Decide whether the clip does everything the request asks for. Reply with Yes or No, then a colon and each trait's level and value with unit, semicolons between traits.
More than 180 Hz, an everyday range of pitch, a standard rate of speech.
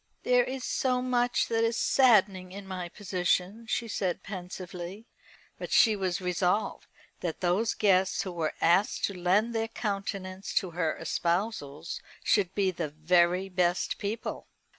Yes: high, 190 Hz; average, 3.5 semitones; average, 145 wpm